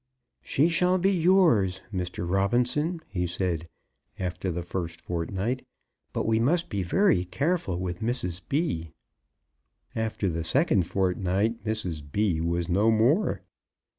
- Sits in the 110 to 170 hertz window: No, low, 100 Hz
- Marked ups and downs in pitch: Yes, wide, 7.2 semitones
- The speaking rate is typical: No, slow, 130 wpm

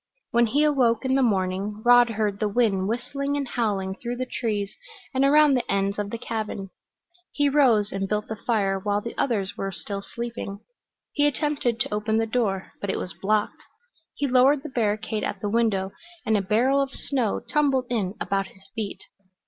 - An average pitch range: Yes, average, 4.1 semitones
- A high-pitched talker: Yes, high, 220 Hz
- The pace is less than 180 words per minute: No, average, 190 wpm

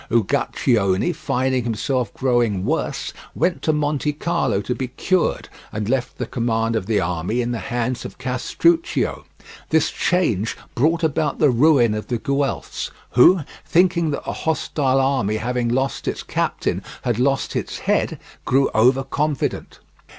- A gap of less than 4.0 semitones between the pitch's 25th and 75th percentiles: No, average, 4.3 semitones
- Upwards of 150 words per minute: No, average, 145 wpm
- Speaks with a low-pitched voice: Yes, low, 130 Hz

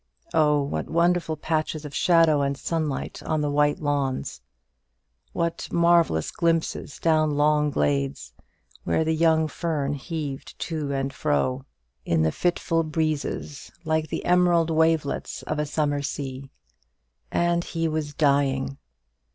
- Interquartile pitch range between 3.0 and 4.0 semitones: No, narrow, 2.6 semitones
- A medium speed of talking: No, slow, 130 wpm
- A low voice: No, medium, 150 Hz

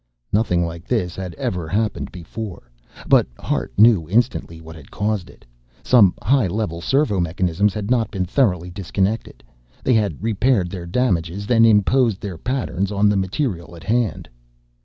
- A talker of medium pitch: No, low, 100 Hz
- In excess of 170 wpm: No, average, 160 wpm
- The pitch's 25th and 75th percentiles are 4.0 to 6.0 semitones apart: Yes, average, 4.3 semitones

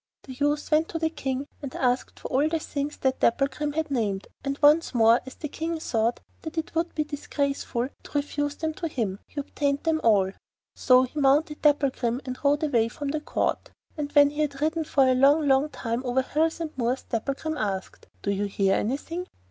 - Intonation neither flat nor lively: Yes, average, 3.3 semitones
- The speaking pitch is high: Yes, very high, 280 Hz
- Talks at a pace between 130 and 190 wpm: No, fast, 205 wpm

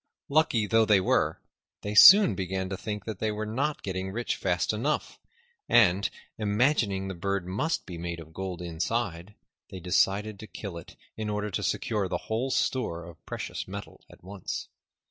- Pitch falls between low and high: No, low, 100 Hz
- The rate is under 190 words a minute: Yes, average, 170 wpm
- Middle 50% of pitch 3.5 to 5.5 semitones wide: No, average, 3.0 semitones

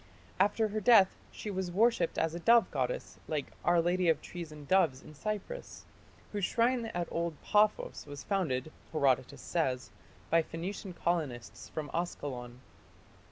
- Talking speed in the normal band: Yes, average, 150 wpm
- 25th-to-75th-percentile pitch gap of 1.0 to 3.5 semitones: No, average, 5.2 semitones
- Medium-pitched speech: Yes, medium, 175 Hz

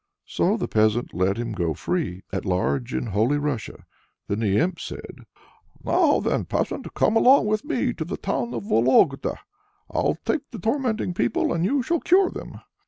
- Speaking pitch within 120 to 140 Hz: Yes, low, 135 Hz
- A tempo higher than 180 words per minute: No, average, 175 wpm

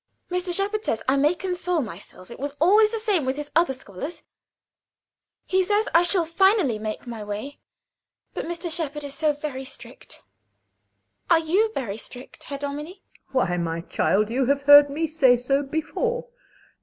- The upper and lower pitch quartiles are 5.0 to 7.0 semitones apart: Yes, wide, 5.5 semitones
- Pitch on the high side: Yes, very high, 290 Hz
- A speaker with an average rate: Yes, average, 170 wpm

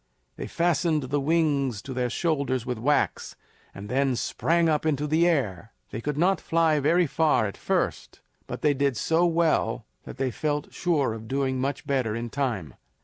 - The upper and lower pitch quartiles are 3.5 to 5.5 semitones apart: Yes, average, 4.2 semitones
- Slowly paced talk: No, average, 180 wpm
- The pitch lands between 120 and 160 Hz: Yes, medium, 140 Hz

